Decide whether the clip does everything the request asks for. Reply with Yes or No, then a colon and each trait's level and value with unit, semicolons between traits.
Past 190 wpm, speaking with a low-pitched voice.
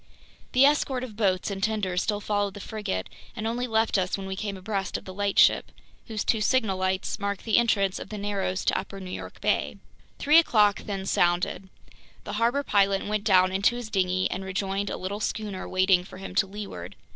No: fast, 205 wpm; high, 200 Hz